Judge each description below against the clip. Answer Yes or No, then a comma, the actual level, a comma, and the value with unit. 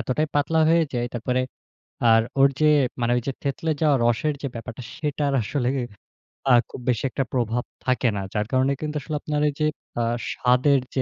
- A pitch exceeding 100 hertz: Yes, low, 135 Hz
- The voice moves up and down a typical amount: Yes, average, 3.3 semitones